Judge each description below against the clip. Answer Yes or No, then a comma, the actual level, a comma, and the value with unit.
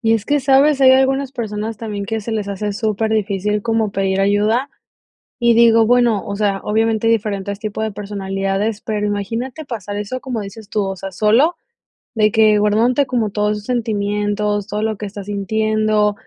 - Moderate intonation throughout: No, narrow, 1.9 semitones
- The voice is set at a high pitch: Yes, high, 215 Hz